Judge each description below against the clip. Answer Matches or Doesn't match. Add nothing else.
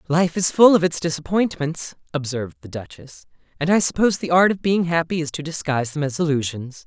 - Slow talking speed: Doesn't match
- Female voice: Doesn't match